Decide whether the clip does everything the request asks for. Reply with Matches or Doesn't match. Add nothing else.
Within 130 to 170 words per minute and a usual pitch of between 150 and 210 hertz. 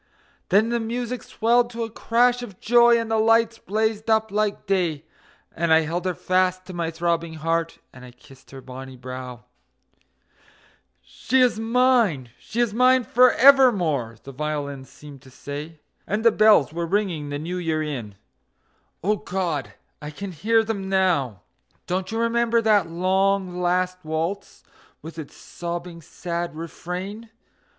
Matches